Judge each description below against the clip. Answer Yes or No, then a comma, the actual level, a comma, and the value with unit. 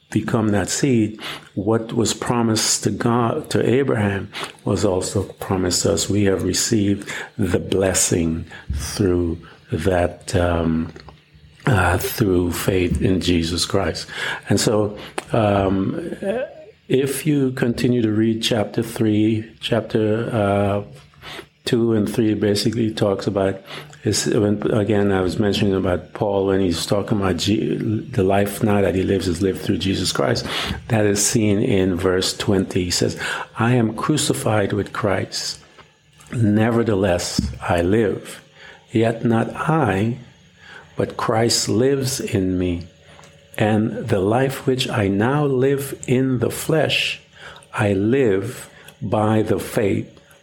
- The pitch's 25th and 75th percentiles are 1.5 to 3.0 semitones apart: No, average, 3.5 semitones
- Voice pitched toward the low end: Yes, low, 105 Hz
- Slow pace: Yes, slow, 130 wpm